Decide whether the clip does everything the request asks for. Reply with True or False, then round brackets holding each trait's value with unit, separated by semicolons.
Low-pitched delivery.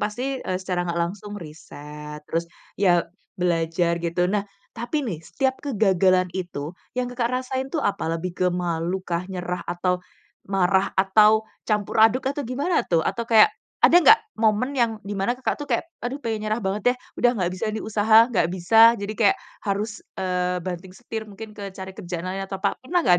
False (195 Hz)